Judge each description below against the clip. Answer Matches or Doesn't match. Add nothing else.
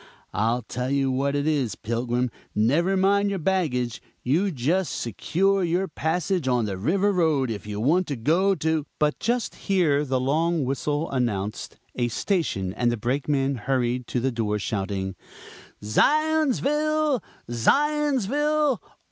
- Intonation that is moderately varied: Doesn't match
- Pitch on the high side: Doesn't match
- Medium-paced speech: Matches